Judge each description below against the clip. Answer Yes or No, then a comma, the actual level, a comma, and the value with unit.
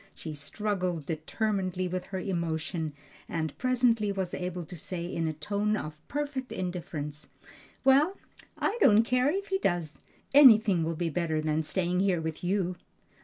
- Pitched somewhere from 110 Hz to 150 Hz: No, medium, 180 Hz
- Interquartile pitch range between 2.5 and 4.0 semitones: No, average, 4.9 semitones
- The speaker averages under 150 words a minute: No, average, 155 wpm